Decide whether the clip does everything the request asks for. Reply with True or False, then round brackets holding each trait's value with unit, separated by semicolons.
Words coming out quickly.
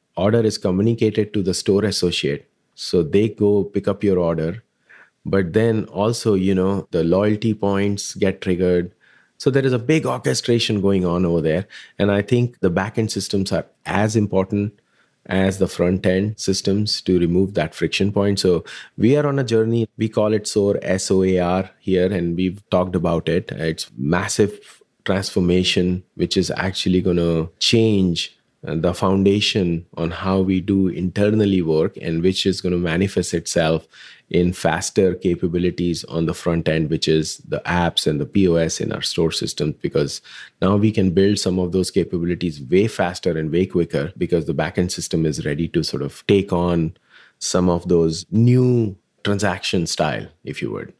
False (175 wpm)